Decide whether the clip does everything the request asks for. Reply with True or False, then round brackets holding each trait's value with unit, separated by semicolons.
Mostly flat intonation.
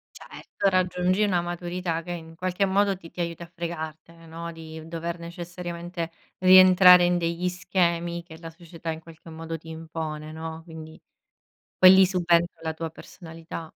True (1.6 semitones)